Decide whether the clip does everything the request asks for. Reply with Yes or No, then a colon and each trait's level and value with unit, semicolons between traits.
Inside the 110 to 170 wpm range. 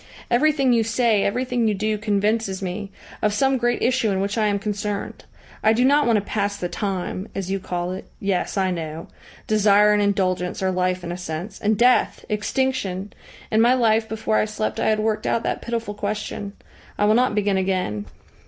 No: average, 200 wpm